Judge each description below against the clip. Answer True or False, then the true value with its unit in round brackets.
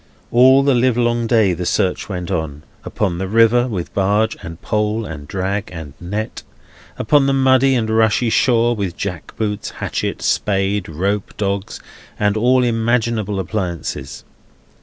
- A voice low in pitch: True (105 Hz)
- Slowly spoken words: False (145 wpm)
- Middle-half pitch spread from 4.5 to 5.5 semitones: False (3.8 semitones)